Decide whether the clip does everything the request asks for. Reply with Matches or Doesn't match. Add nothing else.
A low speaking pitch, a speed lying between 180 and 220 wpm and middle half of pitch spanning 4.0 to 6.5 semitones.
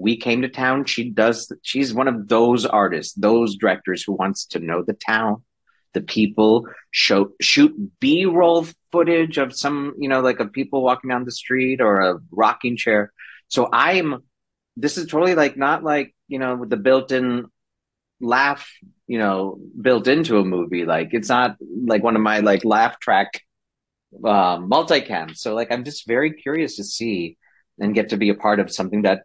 Matches